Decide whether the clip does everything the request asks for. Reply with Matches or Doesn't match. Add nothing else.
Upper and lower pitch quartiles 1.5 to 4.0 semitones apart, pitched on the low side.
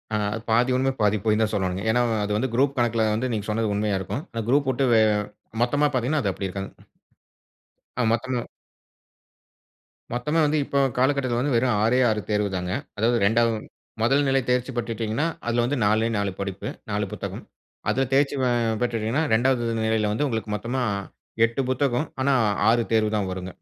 Matches